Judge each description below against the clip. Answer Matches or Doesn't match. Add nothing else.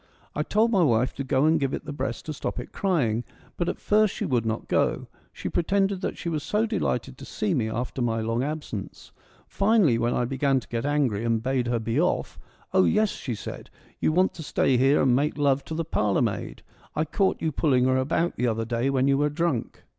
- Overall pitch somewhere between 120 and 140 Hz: Matches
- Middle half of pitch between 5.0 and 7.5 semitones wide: Matches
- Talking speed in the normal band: Doesn't match